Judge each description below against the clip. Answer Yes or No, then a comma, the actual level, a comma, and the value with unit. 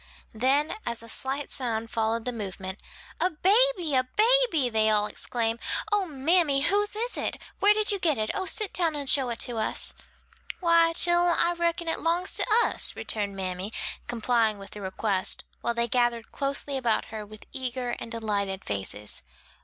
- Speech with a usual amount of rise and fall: No, wide, 7.4 semitones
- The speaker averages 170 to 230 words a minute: Yes, average, 175 wpm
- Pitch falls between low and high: No, very high, 250 Hz